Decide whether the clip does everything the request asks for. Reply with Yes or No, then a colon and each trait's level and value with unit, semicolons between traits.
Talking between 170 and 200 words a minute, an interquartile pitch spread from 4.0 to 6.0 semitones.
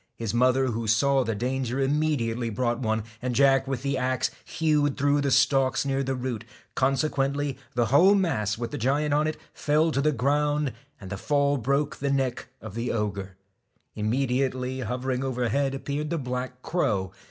No: average, 175 wpm; average, 2.9 semitones